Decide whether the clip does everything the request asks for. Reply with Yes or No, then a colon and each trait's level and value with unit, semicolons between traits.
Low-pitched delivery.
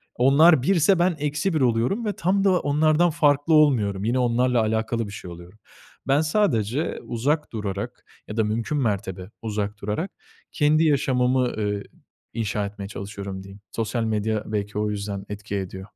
Yes: low, 115 Hz